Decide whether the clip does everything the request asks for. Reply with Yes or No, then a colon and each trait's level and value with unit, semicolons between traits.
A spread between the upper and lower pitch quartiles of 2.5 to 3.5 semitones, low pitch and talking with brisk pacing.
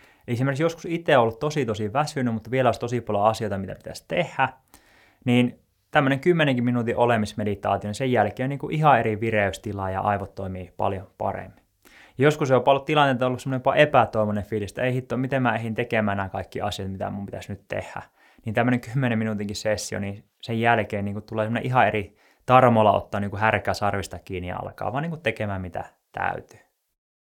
No: average, 4.0 semitones; low, 110 Hz; fast, 185 wpm